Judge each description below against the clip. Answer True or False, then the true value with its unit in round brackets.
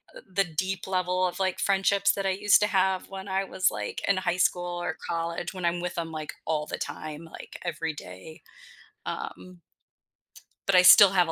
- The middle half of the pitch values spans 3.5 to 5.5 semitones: False (2.5 semitones)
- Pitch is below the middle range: False (180 Hz)